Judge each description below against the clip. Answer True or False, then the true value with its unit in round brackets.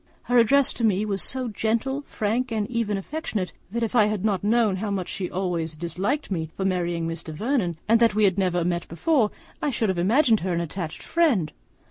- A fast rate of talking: True (215 wpm)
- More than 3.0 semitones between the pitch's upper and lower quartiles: True (4.6 semitones)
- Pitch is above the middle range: True (205 Hz)